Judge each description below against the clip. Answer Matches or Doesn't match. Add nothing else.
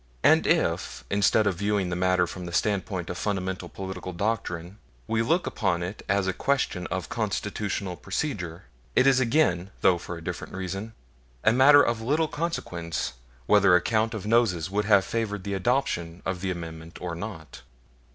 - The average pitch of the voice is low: Matches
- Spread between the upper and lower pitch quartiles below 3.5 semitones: Doesn't match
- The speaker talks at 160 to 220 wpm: Matches